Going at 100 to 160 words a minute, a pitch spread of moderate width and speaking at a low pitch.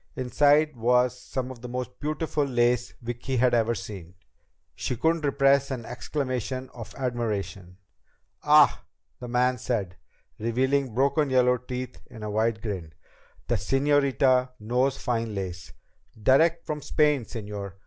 Yes: slow, 135 wpm; average, 3.0 semitones; low, 125 Hz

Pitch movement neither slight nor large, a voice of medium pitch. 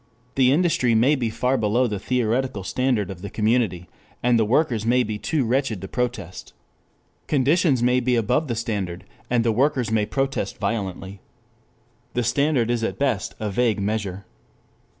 No: average, 3.5 semitones; low, 115 Hz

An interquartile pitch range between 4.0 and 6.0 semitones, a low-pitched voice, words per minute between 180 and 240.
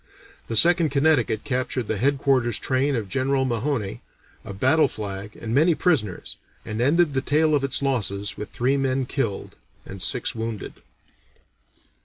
No: average, 4.3 semitones; low, 130 Hz; average, 150 wpm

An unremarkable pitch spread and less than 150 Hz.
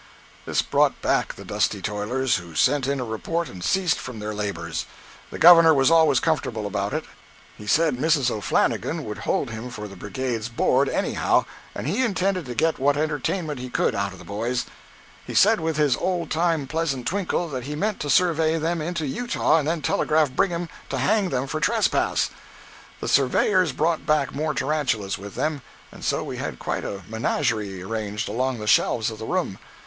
No: wide, 6.6 semitones; medium, 140 Hz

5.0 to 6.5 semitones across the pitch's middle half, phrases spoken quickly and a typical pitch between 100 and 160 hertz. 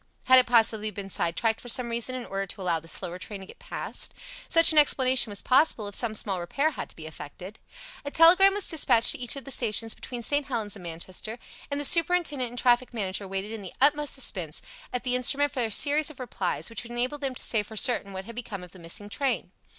No: wide, 5.4 semitones; fast, 240 wpm; high, 235 Hz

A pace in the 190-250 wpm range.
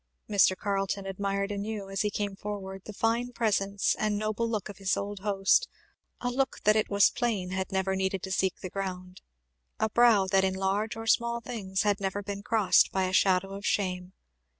Yes: average, 195 wpm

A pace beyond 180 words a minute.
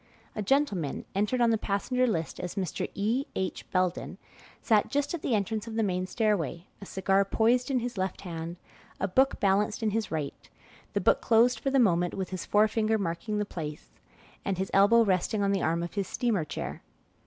Yes: average, 200 wpm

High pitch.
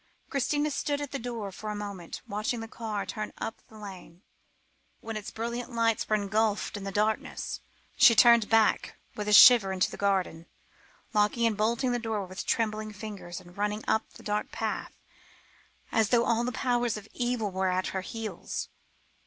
Yes: high, 215 Hz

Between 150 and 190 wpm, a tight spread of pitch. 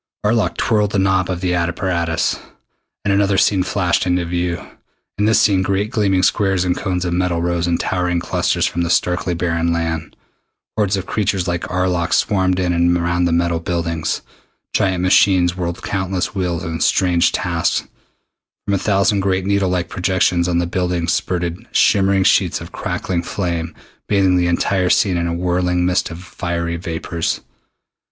Yes: average, 170 wpm; narrow, 1.8 semitones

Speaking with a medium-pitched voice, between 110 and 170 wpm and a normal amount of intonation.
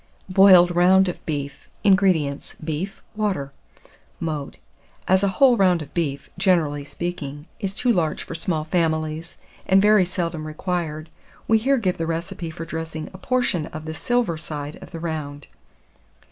Yes: medium, 170 Hz; average, 160 wpm; average, 3.5 semitones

